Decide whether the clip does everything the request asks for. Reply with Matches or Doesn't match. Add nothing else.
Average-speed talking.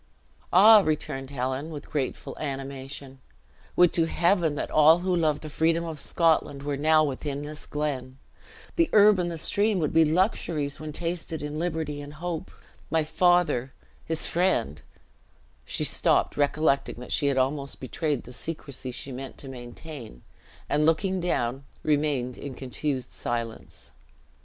Matches